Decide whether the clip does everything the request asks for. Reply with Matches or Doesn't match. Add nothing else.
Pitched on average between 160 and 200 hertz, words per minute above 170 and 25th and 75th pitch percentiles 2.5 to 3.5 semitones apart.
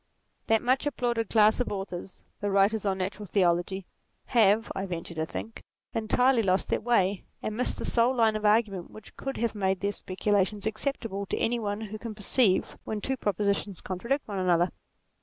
Doesn't match